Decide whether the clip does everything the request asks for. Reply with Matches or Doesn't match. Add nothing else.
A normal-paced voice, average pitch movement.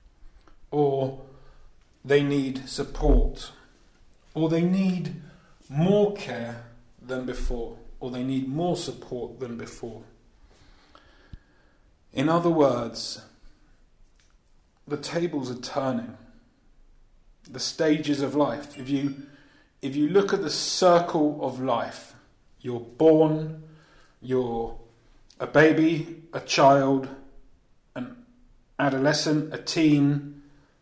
Doesn't match